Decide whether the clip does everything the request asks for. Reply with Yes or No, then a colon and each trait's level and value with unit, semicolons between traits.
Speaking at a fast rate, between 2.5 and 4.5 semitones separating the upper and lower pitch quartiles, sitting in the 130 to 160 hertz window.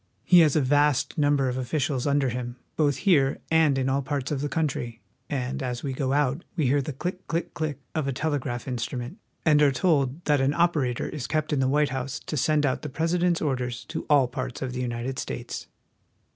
Yes: fast, 215 wpm; average, 2.9 semitones; medium, 140 Hz